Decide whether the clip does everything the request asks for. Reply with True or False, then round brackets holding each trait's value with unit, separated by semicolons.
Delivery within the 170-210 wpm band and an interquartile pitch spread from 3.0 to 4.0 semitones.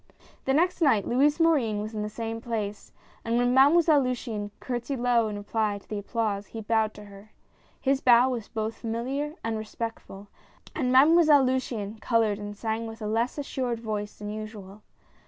True (180 wpm; 3.4 semitones)